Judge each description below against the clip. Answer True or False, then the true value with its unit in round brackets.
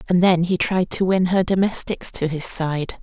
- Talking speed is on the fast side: True (220 wpm)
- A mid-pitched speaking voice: True (180 Hz)